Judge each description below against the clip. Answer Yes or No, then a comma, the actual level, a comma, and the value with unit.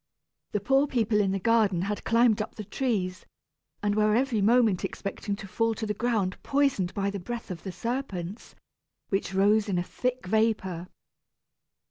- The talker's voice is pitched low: No, high, 210 Hz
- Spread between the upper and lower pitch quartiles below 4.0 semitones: Yes, average, 3.2 semitones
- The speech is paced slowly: No, average, 170 wpm